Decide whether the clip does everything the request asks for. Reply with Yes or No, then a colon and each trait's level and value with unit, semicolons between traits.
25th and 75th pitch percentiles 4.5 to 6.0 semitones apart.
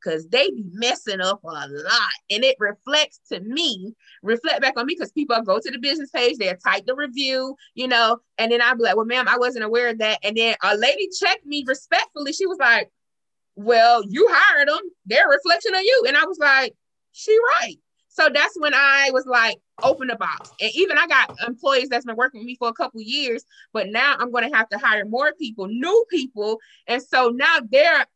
Yes: average, 4.8 semitones